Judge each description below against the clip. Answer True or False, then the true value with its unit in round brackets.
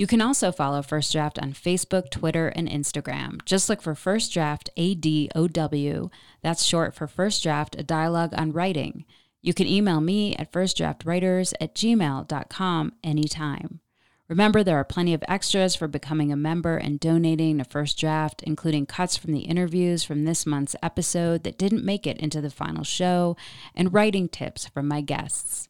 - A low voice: False (165 Hz)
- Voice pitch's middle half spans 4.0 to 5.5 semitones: False (3.3 semitones)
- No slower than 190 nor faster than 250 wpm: False (175 wpm)